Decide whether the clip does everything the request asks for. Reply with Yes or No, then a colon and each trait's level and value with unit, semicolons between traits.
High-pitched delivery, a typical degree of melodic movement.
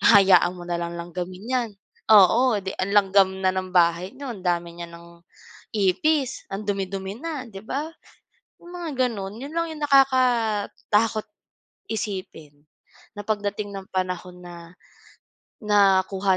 Yes: high, 195 Hz; average, 3.8 semitones